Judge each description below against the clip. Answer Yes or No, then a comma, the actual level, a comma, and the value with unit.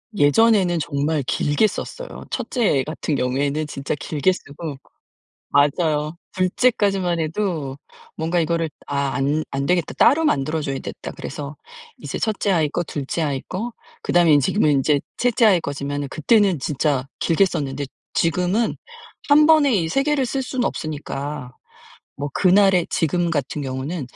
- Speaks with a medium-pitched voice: Yes, medium, 160 Hz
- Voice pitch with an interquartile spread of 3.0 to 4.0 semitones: No, average, 5.2 semitones